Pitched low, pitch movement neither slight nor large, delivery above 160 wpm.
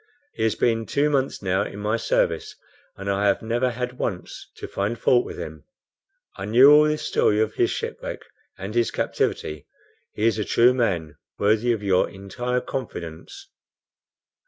Yes: low, 110 Hz; average, 3.9 semitones; average, 170 wpm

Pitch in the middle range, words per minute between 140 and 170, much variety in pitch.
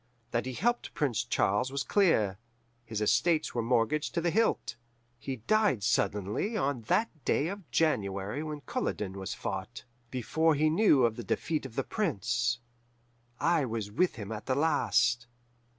No: low, 130 Hz; average, 160 wpm; wide, 6.5 semitones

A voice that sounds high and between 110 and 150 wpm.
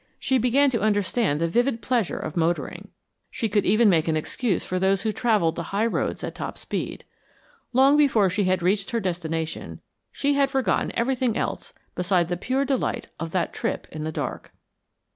No: high, 205 Hz; average, 185 wpm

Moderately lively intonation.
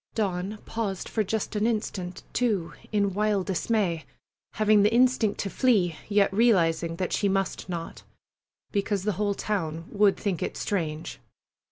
Yes: average, 3.0 semitones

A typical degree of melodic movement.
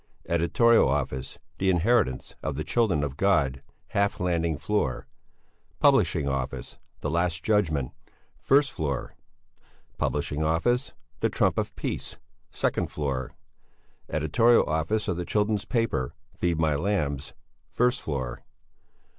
No: wide, 6.6 semitones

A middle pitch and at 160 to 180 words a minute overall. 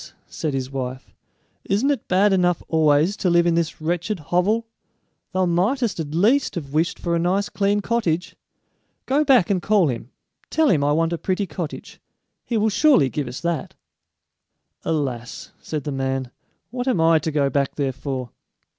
Yes: medium, 170 Hz; average, 175 wpm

